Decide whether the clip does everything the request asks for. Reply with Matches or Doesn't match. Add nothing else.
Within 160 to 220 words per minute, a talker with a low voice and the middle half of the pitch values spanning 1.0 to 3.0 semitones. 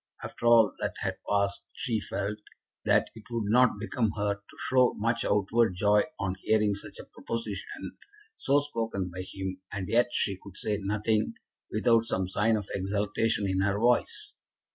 Matches